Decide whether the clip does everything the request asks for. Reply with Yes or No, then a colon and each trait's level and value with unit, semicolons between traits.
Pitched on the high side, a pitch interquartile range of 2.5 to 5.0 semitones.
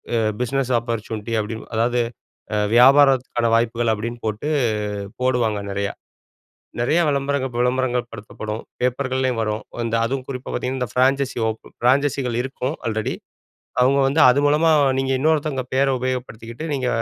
No: low, 125 Hz; average, 2.8 semitones